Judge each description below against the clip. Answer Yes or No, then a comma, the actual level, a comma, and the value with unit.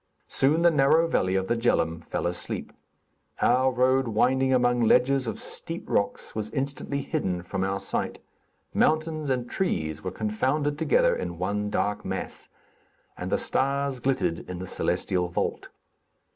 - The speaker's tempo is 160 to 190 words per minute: No, average, 150 wpm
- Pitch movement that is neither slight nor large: No, wide, 6.2 semitones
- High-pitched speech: No, low, 125 Hz